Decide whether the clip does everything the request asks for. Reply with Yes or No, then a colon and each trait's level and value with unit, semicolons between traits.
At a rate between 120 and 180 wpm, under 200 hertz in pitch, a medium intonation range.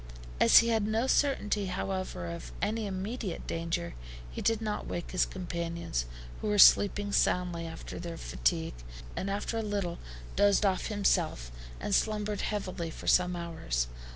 Yes: average, 155 wpm; high, 190 Hz; average, 3.6 semitones